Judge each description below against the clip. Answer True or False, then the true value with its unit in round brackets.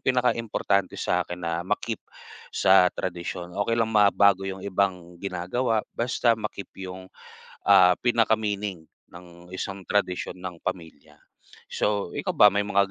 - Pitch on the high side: False (95 Hz)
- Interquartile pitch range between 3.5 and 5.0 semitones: False (2.6 semitones)